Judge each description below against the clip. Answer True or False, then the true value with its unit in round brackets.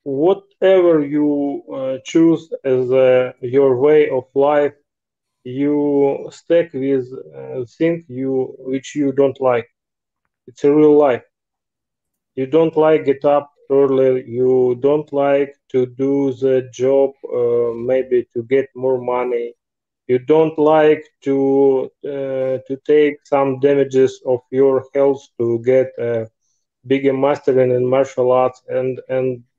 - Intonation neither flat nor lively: False (2.1 semitones)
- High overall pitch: False (135 Hz)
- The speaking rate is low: True (130 wpm)